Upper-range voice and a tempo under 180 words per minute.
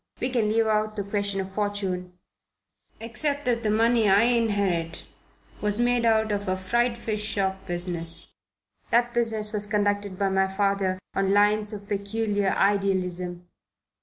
Yes: high, 205 Hz; average, 150 wpm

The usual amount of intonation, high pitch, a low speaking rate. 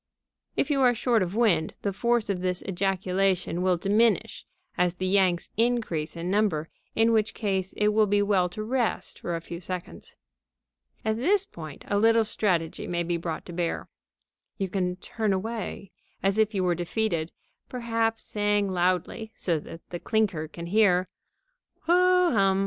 No: average, 3.7 semitones; high, 195 Hz; average, 165 wpm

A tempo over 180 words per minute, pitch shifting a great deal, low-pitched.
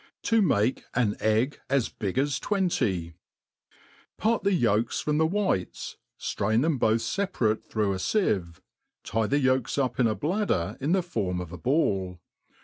No: average, 160 wpm; wide, 7.6 semitones; low, 120 Hz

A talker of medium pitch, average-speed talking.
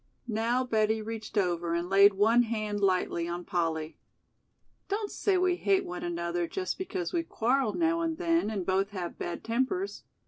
No: high, 215 Hz; average, 170 wpm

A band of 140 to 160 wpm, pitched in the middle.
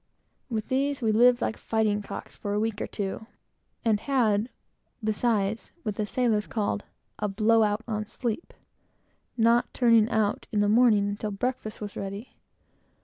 No: average, 155 wpm; high, 220 Hz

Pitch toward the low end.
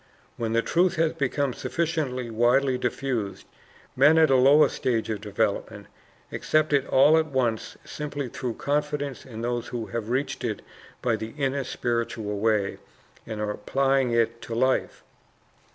Yes: low, 125 Hz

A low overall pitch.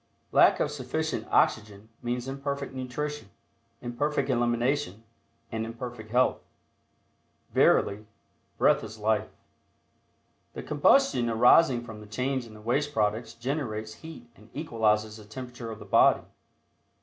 Yes: low, 120 Hz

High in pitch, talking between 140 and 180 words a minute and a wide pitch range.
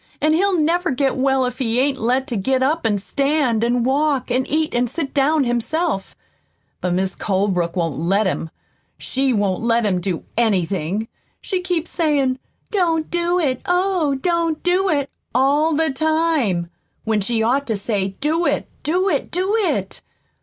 Yes: very high, 265 Hz; average, 170 wpm; wide, 6.4 semitones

